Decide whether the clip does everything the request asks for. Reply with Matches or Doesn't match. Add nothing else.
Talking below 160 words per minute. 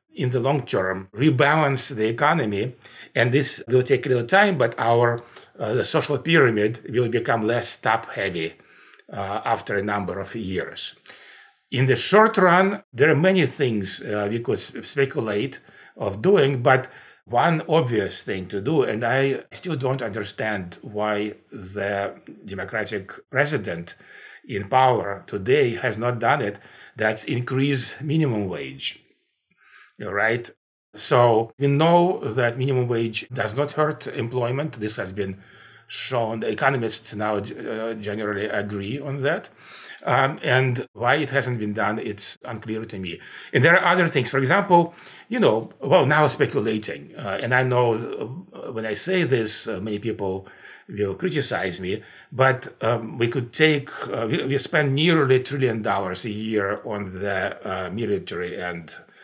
Matches